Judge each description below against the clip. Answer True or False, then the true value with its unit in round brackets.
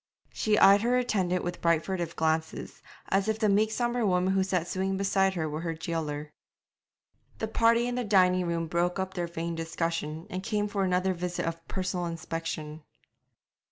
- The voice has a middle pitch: True (180 Hz)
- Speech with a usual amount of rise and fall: True (3.1 semitones)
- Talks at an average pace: True (180 wpm)